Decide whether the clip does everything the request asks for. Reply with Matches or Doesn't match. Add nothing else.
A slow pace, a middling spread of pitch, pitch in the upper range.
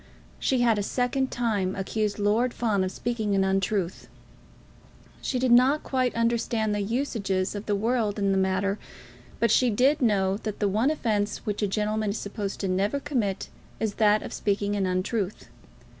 Doesn't match